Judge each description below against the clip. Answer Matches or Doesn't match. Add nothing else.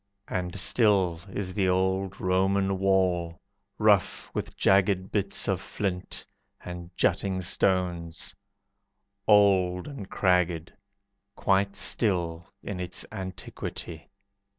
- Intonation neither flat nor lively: Doesn't match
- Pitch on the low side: Matches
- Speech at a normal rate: Doesn't match